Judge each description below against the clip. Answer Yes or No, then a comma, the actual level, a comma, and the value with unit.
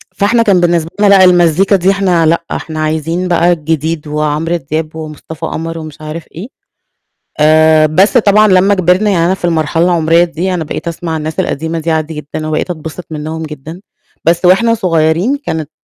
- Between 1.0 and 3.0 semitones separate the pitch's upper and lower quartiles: Yes, narrow, 2.6 semitones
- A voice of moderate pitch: Yes, medium, 165 Hz